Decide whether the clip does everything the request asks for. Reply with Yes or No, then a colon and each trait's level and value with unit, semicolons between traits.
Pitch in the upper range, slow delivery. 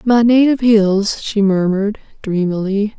Yes: high, 210 Hz; slow, 120 wpm